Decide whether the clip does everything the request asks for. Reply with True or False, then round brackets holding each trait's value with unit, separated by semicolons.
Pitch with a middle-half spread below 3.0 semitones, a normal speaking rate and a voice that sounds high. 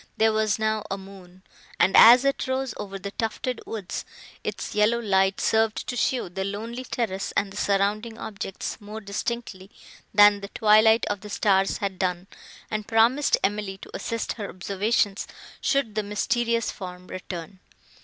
True (2.5 semitones; 160 wpm; 210 Hz)